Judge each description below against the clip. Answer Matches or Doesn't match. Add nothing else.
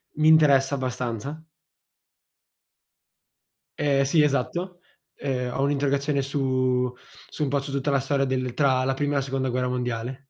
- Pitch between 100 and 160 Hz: Matches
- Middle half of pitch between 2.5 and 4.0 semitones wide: Doesn't match